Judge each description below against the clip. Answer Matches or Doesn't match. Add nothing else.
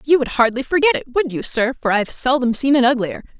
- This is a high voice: Matches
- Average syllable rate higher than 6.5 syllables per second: Doesn't match